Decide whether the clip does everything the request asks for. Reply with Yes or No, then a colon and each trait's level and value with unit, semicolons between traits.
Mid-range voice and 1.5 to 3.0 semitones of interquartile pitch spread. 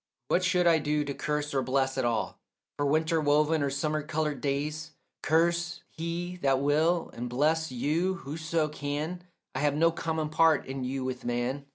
Yes: medium, 150 Hz; average, 2.7 semitones